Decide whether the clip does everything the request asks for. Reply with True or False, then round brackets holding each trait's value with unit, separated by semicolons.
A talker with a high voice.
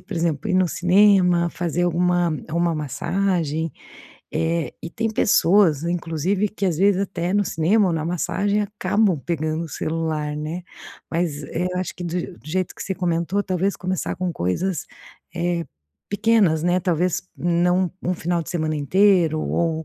False (175 Hz)